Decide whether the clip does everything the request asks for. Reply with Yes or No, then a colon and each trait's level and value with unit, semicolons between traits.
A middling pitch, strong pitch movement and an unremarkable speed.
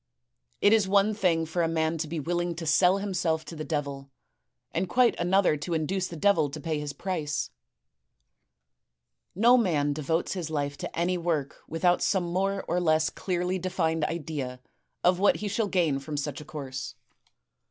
No: medium, 165 Hz; average, 3.6 semitones; average, 180 wpm